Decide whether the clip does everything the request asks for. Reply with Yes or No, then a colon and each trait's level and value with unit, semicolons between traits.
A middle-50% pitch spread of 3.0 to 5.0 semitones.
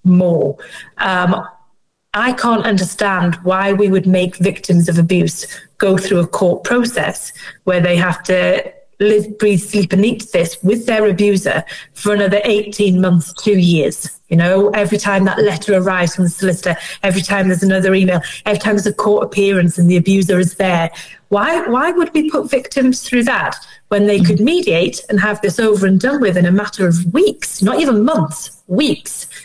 No: narrow, 2.6 semitones